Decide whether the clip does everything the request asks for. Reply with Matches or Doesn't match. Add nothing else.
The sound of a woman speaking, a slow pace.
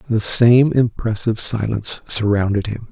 Doesn't match